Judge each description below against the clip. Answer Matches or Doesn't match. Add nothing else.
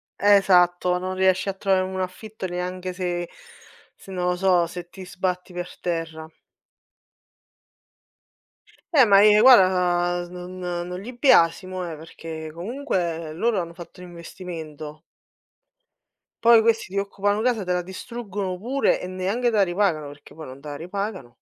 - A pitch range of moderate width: Doesn't match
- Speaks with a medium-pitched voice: Matches